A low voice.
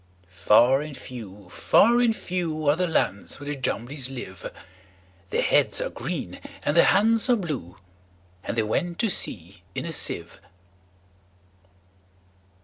Yes: low, 125 Hz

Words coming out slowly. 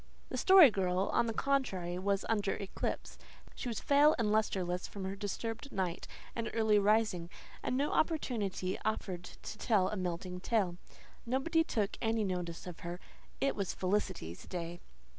No: average, 160 wpm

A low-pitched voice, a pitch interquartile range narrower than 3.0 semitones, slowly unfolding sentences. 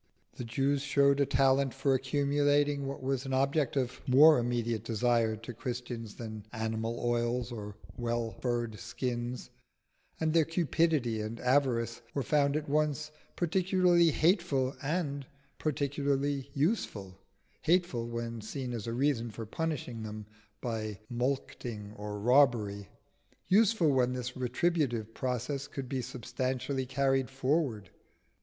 No: low, 130 Hz; average, 3.4 semitones; slow, 130 wpm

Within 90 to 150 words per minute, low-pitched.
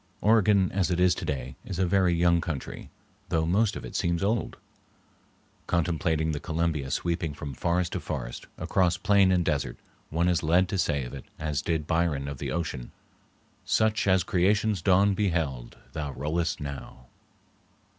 No: average, 165 wpm; very low, 85 Hz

